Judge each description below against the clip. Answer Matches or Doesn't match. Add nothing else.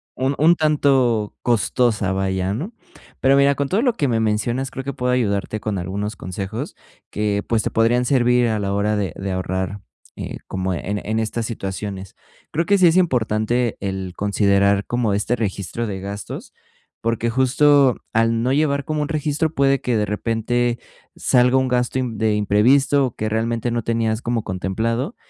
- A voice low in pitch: Matches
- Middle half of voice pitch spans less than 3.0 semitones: Doesn't match